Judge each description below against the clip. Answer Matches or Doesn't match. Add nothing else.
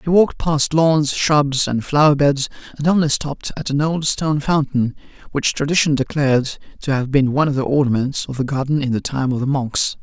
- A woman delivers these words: Doesn't match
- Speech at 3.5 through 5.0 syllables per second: Doesn't match